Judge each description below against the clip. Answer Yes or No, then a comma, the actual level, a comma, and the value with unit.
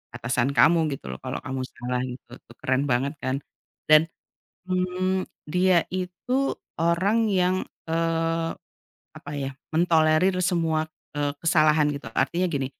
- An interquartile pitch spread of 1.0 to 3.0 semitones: No, average, 4.3 semitones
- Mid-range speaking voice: Yes, medium, 165 Hz